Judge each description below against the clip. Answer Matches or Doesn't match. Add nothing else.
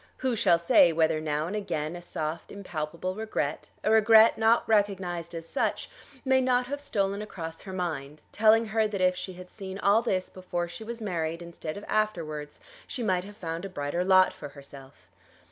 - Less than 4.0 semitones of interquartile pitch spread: Doesn't match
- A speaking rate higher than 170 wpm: Matches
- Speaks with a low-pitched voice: Doesn't match